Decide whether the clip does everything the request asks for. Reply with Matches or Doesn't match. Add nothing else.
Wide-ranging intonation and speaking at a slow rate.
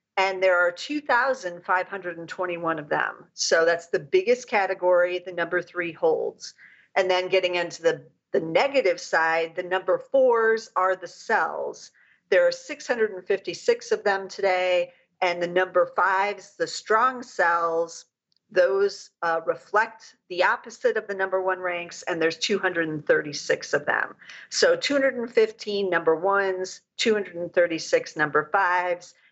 Doesn't match